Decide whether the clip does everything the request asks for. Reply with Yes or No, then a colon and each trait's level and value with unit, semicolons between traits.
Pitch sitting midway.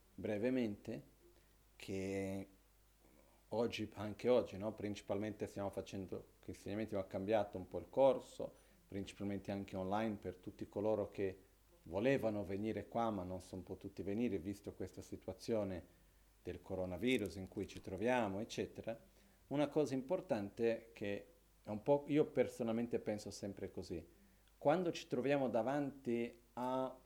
No: low, 100 Hz